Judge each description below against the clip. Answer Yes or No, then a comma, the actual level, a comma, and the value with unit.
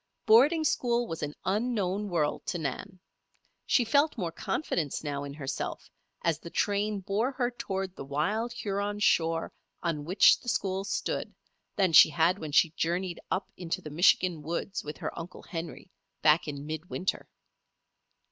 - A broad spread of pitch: No, average, 4.6 semitones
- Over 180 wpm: No, average, 160 wpm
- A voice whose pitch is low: No, medium, 180 Hz